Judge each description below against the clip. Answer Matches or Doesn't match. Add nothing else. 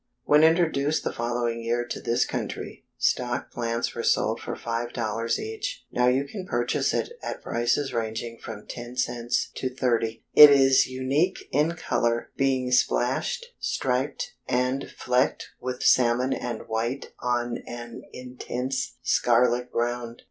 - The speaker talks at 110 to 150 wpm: Matches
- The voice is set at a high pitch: Doesn't match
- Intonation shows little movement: Matches